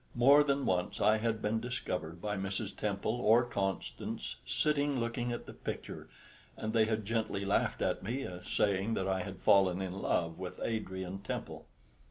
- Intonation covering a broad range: No, average, 3.6 semitones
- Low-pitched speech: Yes, low, 105 Hz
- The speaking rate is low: No, average, 170 wpm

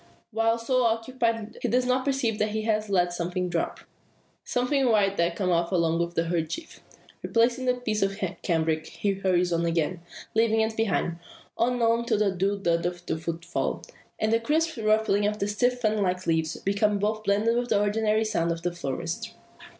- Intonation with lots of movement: No, average, 4.6 semitones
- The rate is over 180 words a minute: Yes, average, 190 wpm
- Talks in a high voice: Yes, high, 210 Hz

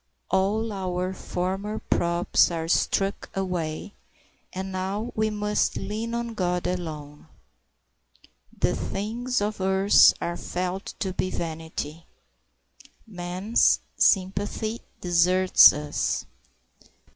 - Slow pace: Yes, slow, 100 wpm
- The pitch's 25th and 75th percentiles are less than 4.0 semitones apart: Yes, average, 2.9 semitones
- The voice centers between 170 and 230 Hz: Yes, high, 190 Hz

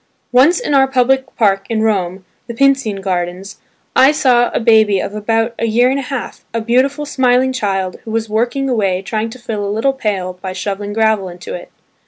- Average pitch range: Yes, average, 4.3 semitones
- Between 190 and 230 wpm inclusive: Yes, average, 200 wpm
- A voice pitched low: No, high, 225 Hz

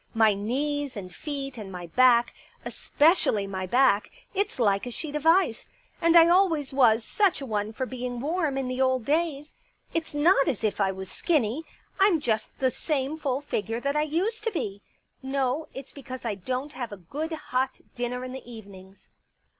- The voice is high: Yes, very high, 260 Hz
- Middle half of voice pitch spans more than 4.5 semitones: Yes, average, 5.2 semitones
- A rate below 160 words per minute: No, average, 195 wpm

